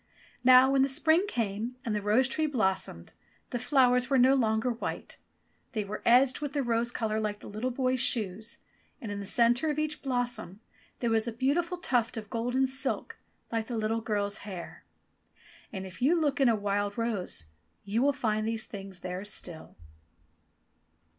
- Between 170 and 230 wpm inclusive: Yes, average, 175 wpm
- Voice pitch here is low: No, high, 235 Hz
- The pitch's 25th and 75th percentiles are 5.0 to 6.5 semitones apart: No, average, 3.7 semitones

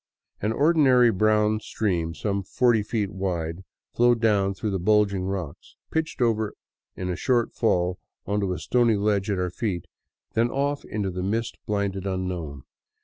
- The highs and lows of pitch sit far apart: No, average, 3.4 semitones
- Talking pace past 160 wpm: No, average, 155 wpm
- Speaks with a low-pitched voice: Yes, low, 100 Hz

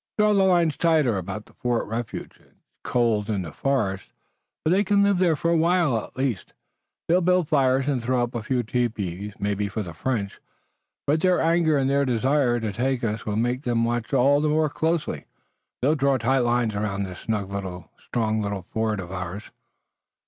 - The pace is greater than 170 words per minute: Yes, average, 190 wpm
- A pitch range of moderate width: No, wide, 6.0 semitones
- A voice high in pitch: No, low, 120 Hz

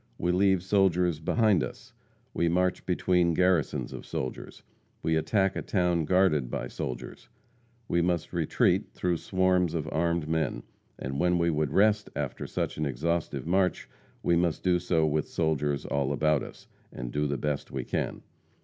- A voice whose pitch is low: Yes, very low, 85 Hz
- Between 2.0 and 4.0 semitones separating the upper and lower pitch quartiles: Yes, average, 3.2 semitones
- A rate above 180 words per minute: No, average, 165 wpm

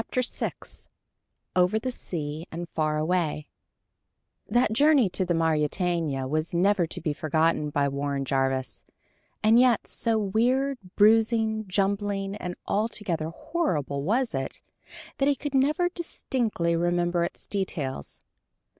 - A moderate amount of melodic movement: No, wide, 6.3 semitones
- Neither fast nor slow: No, slow, 130 wpm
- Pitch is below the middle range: No, medium, 180 Hz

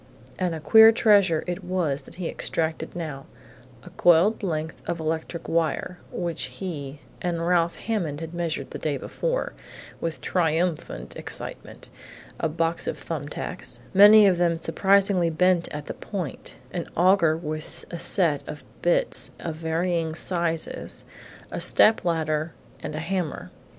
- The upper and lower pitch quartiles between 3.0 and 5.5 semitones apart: No, narrow, 2.4 semitones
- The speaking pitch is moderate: Yes, medium, 170 Hz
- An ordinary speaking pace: Yes, average, 145 wpm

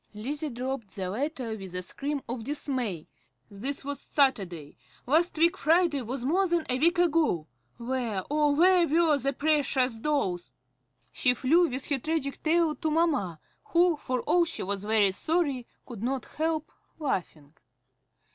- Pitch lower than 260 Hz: No, very high, 275 Hz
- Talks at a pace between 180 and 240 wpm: No, average, 155 wpm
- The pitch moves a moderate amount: No, wide, 5.8 semitones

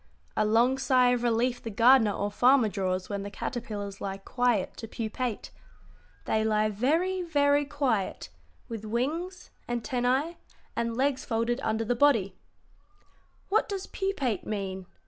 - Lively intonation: No, average, 4.2 semitones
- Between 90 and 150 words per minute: Yes, average, 140 wpm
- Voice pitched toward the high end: Yes, high, 240 Hz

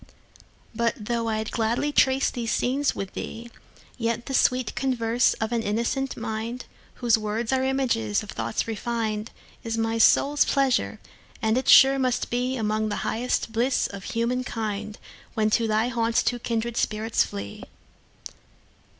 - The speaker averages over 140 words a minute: No, slow, 135 wpm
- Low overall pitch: No, high, 230 Hz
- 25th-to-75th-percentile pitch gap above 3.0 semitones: No, narrow, 2.4 semitones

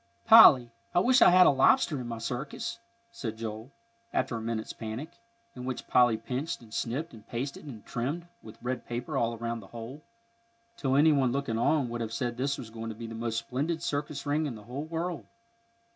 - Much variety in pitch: No, average, 4.1 semitones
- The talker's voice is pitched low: Yes, low, 125 Hz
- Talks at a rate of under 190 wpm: No, fast, 205 wpm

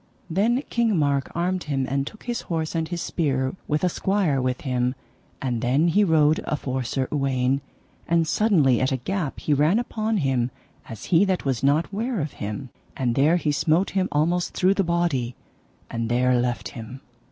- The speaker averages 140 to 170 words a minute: No, average, 185 wpm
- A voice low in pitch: No, medium, 150 Hz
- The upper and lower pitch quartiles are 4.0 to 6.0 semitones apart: Yes, average, 5.3 semitones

